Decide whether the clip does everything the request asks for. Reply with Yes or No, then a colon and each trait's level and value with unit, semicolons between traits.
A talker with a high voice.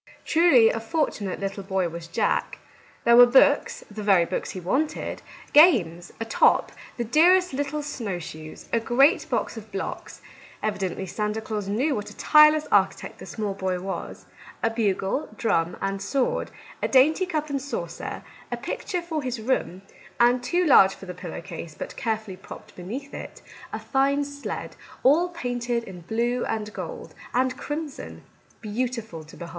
Yes: high, 230 Hz